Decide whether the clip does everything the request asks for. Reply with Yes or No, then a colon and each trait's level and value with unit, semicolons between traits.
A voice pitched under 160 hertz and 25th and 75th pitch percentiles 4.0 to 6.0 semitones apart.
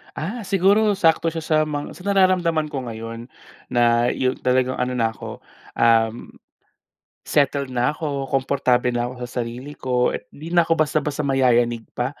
Yes: low, 135 Hz; average, 4.8 semitones